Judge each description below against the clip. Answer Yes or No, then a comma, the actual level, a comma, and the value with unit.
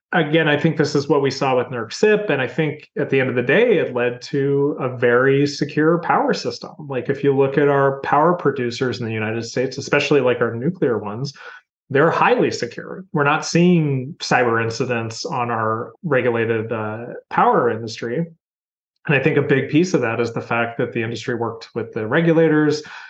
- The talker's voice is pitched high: No, low, 135 Hz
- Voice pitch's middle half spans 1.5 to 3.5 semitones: No, average, 4.3 semitones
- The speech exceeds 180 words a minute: Yes, average, 200 wpm